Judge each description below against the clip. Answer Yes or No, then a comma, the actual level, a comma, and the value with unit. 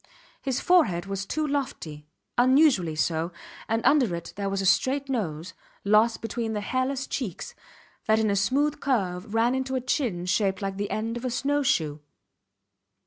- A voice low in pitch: No, high, 225 Hz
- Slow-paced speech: No, average, 170 wpm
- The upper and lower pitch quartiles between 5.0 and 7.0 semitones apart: Yes, wide, 5.5 semitones